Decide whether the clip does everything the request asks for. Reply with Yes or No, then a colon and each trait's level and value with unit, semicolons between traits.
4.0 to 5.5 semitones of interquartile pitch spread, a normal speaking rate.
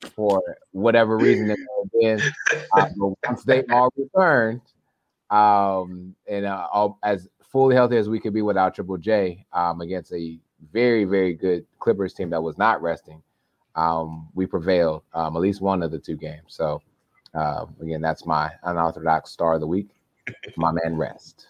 Yes: average, 5.2 semitones; average, 165 wpm